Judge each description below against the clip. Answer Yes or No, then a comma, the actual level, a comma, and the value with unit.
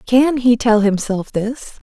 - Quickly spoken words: No, average, 160 wpm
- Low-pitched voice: No, high, 230 Hz